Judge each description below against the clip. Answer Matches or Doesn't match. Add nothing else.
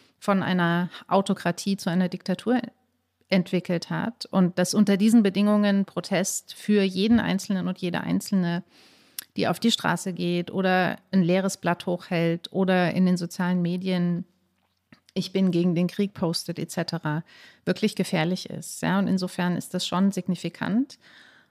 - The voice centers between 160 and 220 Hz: Matches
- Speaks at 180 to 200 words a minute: Doesn't match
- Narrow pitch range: Matches